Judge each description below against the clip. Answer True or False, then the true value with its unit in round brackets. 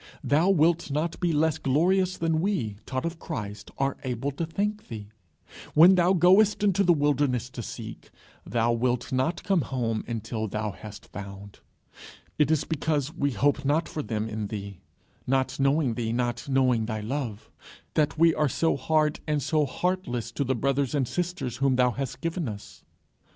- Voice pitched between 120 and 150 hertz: True (140 Hz)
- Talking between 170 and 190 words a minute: True (175 wpm)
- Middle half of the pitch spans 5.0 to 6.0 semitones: True (5.5 semitones)